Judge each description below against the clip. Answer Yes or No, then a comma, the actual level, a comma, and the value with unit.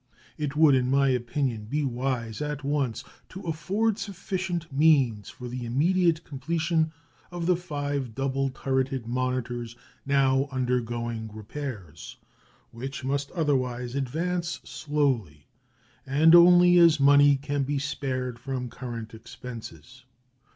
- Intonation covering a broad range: No, average, 3.5 semitones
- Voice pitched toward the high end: No, low, 135 Hz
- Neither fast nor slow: No, slow, 120 wpm